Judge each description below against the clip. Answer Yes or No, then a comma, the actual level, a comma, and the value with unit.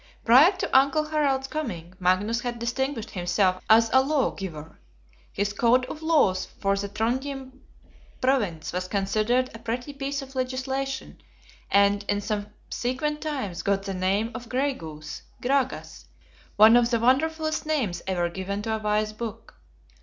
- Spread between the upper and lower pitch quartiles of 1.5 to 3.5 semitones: No, average, 5.1 semitones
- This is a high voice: Yes, high, 235 Hz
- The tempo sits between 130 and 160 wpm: Yes, average, 145 wpm